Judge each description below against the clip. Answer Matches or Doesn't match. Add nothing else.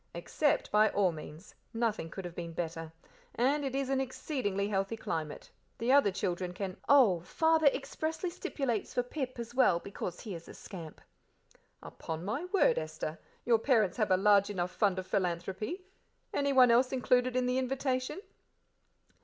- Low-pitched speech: Doesn't match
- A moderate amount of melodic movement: Doesn't match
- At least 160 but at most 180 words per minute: Matches